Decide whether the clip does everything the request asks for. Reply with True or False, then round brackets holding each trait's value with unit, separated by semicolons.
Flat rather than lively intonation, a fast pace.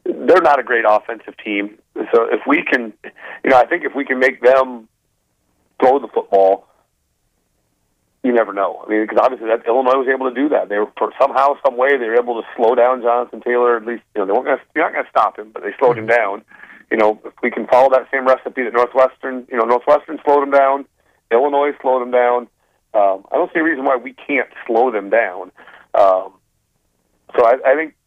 False (4.2 semitones; 225 wpm)